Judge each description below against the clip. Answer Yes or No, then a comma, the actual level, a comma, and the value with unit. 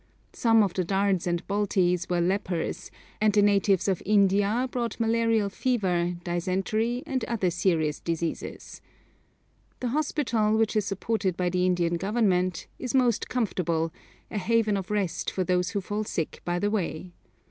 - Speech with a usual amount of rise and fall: Yes, average, 3.6 semitones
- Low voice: No, high, 195 Hz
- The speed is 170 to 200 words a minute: No, average, 155 wpm